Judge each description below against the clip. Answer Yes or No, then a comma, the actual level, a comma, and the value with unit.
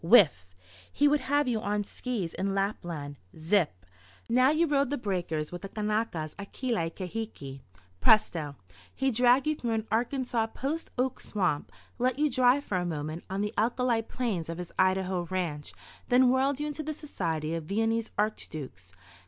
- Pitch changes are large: Yes, wide, 6.6 semitones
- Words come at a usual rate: Yes, average, 165 wpm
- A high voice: Yes, high, 215 Hz